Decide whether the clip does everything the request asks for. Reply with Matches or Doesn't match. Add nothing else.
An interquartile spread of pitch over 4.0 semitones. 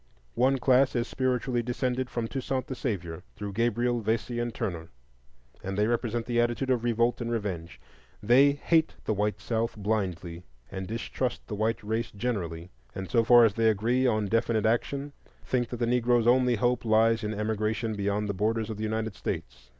Doesn't match